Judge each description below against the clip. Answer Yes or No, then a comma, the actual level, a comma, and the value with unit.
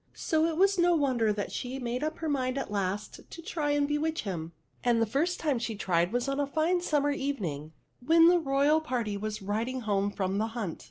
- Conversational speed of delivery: No, fast, 225 wpm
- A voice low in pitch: No, very high, 260 Hz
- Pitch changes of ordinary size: No, wide, 6.7 semitones